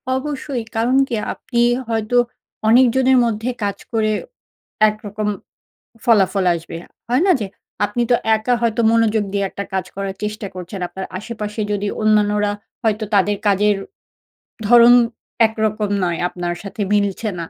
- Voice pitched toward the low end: No, high, 215 Hz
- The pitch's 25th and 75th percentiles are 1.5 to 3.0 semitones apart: Yes, narrow, 2.5 semitones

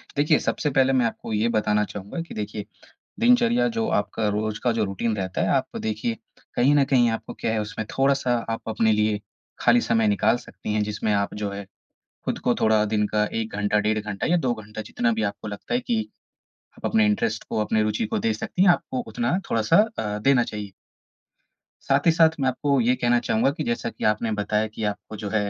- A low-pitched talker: Yes, low, 110 Hz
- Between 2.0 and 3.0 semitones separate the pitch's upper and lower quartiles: No, average, 4.3 semitones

